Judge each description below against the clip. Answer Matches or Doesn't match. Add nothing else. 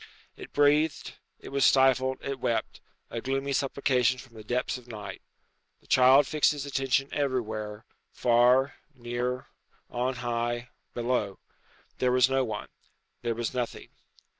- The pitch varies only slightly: Matches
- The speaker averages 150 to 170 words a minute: Doesn't match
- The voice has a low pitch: Matches